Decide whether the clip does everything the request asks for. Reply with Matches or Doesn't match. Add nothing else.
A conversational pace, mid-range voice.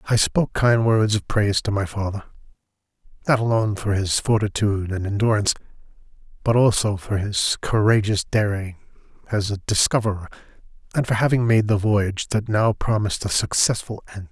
Doesn't match